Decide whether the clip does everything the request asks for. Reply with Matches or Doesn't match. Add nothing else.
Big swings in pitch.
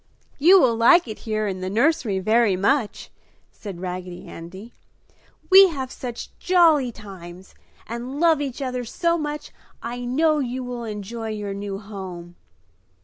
Matches